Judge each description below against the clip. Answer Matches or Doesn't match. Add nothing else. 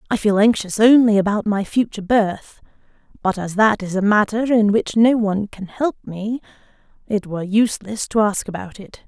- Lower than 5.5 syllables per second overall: Matches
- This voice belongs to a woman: Matches